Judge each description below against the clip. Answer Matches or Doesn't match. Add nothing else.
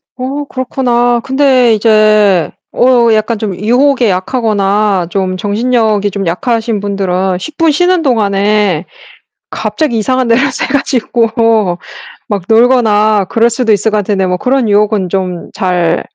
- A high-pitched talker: Matches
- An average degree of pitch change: Matches